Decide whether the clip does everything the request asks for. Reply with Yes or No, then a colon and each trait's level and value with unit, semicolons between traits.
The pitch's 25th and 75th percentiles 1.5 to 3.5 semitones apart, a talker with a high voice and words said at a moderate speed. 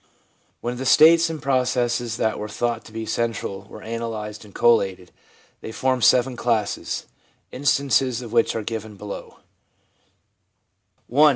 No: average, 2.7 semitones; low, 115 Hz; average, 145 wpm